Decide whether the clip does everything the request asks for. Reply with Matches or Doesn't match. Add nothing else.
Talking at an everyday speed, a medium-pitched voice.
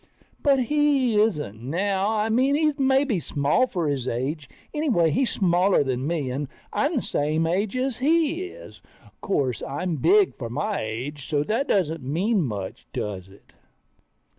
Matches